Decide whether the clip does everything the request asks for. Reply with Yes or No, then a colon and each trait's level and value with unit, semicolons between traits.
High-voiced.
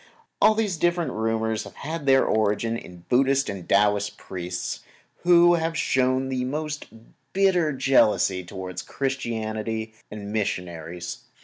No: low, 115 Hz